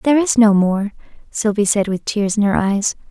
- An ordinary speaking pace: No, fast, 210 wpm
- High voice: Yes, high, 210 Hz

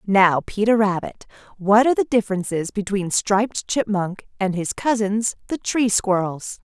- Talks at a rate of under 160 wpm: Yes, average, 145 wpm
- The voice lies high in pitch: Yes, high, 205 Hz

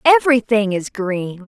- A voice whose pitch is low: No, high, 225 Hz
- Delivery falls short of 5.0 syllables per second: Yes, 4.6 syllables/s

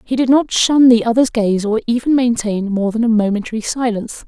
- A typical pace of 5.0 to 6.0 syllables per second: Yes, 5.6 syllables/s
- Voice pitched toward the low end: No, high, 230 Hz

